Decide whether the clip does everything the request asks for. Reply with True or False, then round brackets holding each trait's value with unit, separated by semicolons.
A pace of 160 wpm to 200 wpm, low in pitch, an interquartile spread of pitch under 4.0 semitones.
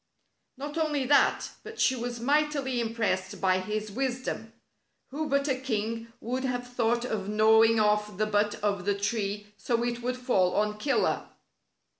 False (165 wpm; 230 Hz; 3.6 semitones)